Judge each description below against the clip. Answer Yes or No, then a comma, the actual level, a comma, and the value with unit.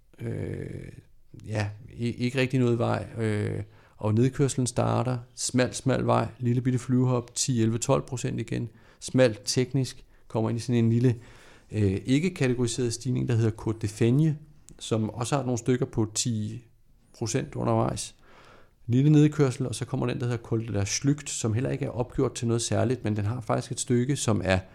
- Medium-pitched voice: No, low, 120 Hz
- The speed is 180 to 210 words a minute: No, average, 170 wpm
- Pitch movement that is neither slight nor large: No, narrow, 2.3 semitones